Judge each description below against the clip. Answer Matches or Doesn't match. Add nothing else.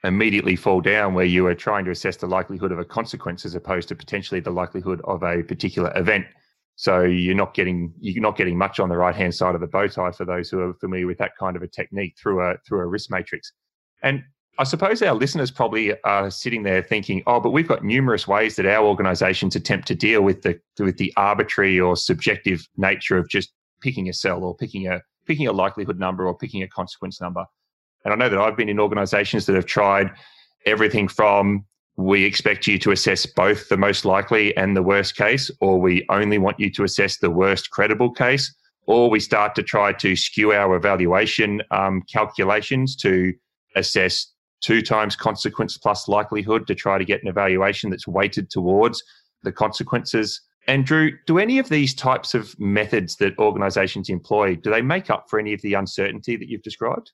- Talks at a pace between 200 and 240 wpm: Matches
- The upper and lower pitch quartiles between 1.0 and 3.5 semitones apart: Matches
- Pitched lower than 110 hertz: Matches